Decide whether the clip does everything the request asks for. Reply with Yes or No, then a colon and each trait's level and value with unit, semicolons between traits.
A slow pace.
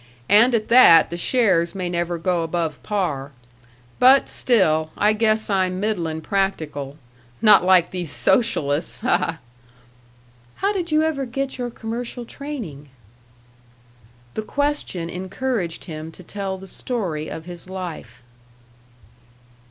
Yes: slow, 130 wpm